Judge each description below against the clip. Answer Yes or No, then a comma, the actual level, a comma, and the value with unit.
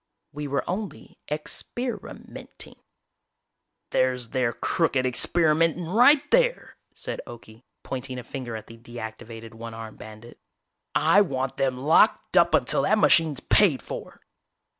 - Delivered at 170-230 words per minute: No, average, 145 wpm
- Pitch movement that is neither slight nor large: No, wide, 6.3 semitones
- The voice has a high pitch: No, low, 135 Hz